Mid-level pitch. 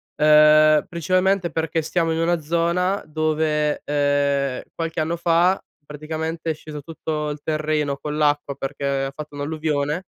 Yes: medium, 155 Hz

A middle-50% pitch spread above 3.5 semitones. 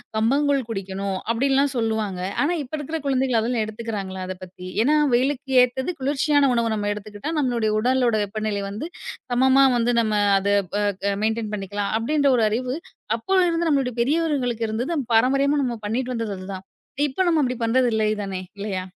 Yes: average, 4.4 semitones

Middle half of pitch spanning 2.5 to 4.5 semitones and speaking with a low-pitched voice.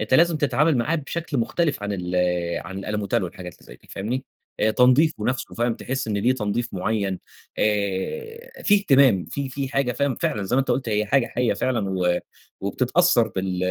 No: average, 5.2 semitones; low, 120 Hz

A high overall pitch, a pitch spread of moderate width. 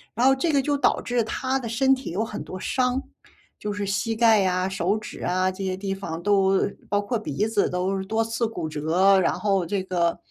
Yes: high, 200 Hz; average, 3.5 semitones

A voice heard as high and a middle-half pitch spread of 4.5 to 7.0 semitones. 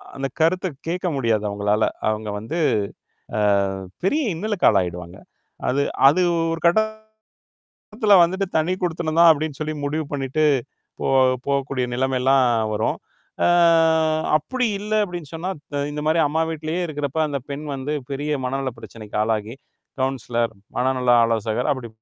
No: medium, 140 Hz; average, 4.9 semitones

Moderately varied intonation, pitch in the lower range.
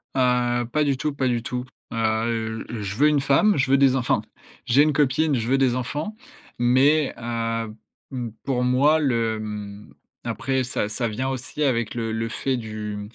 Yes: average, 3.0 semitones; low, 125 Hz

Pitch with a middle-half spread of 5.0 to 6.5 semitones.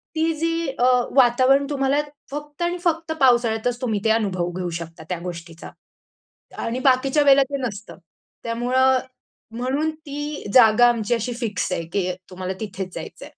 Yes: average, 5.3 semitones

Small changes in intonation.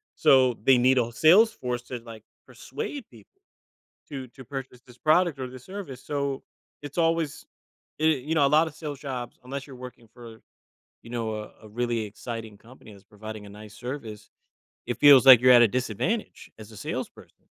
No: average, 3.9 semitones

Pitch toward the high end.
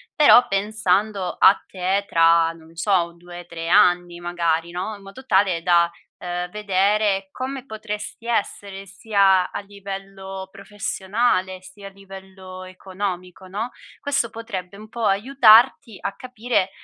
Yes: high, 195 Hz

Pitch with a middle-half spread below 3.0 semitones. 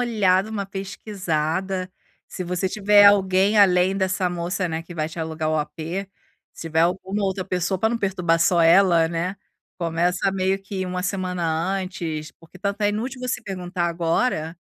Yes: narrow, 2.6 semitones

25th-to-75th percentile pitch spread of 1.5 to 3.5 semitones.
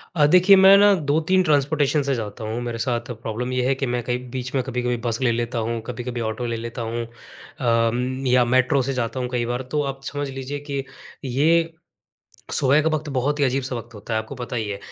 Yes: average, 2.9 semitones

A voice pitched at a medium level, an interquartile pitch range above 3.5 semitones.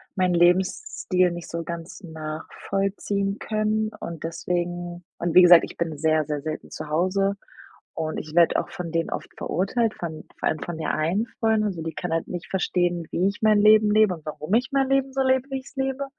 Yes: medium, 180 Hz; average, 4.4 semitones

